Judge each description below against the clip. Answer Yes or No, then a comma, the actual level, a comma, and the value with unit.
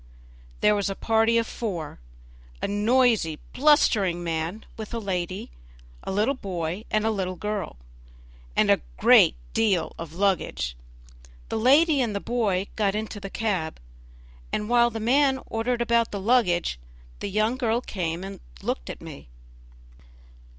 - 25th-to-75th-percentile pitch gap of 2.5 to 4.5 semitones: Yes, average, 4.1 semitones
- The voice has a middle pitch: No, high, 210 Hz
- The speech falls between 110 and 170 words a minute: Yes, average, 150 wpm